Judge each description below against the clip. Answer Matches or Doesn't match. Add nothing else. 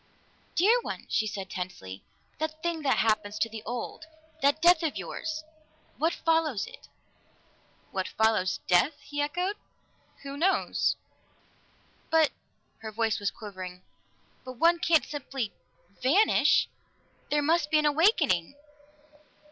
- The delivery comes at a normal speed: Doesn't match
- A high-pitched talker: Matches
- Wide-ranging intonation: Matches